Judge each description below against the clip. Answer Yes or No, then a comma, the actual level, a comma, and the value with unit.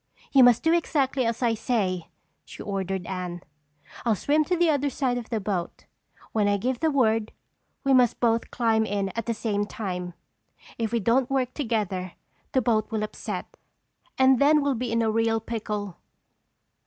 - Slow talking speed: No, average, 180 wpm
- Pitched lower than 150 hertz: No, high, 230 Hz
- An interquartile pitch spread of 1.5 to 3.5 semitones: No, average, 4.0 semitones